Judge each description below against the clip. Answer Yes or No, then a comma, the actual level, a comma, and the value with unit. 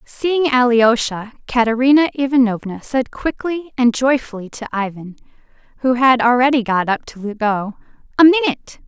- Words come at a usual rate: No, slow, 130 wpm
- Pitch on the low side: No, very high, 250 Hz